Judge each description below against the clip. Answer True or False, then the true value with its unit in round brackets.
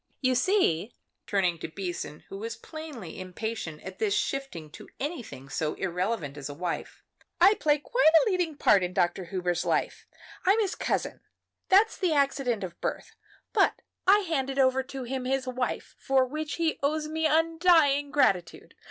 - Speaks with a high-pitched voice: True (260 Hz)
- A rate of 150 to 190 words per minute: True (165 wpm)